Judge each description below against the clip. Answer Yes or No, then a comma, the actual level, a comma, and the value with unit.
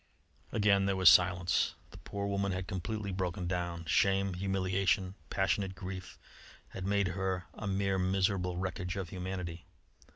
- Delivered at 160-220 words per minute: No, average, 150 wpm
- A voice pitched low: Yes, very low, 95 Hz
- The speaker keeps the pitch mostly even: Yes, narrow, 1.3 semitones